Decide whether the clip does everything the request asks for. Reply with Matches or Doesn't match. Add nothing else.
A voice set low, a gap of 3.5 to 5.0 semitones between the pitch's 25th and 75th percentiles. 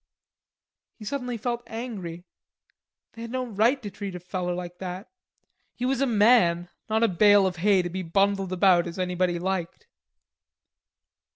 Doesn't match